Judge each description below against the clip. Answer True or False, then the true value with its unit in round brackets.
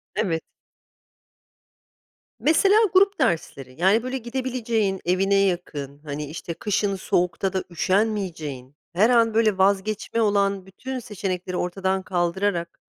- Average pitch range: True (4.0 semitones)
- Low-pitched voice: False (195 Hz)